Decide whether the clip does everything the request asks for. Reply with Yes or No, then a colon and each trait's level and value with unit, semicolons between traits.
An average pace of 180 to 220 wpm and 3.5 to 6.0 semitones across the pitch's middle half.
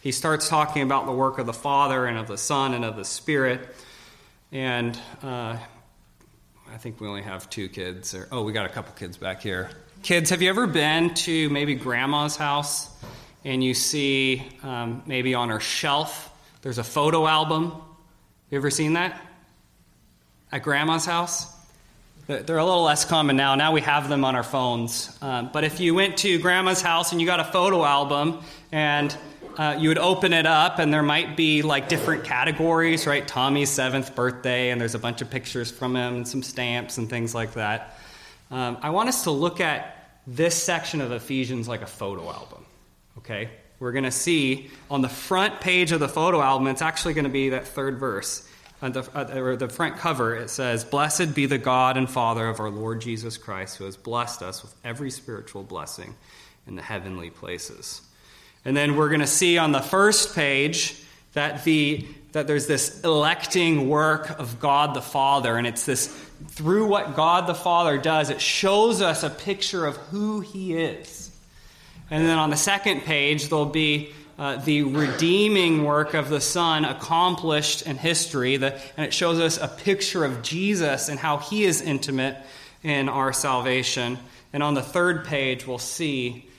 Yes: average, 190 wpm; average, 4.1 semitones